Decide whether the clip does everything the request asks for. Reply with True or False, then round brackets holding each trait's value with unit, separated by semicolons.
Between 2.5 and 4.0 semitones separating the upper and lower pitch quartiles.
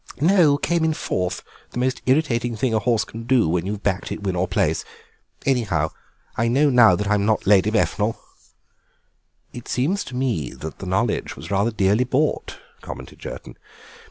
False (4.5 semitones)